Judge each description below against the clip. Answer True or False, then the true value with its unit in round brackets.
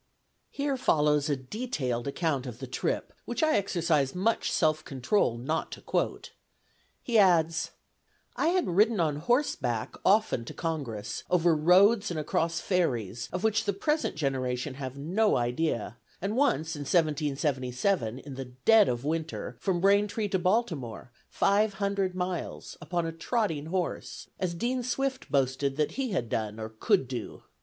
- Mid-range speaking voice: True (165 Hz)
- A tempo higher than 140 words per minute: True (155 wpm)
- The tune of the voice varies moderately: False (7.1 semitones)